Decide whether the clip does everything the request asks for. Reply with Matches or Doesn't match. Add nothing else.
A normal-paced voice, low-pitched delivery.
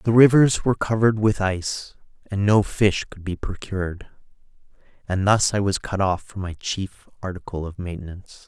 Matches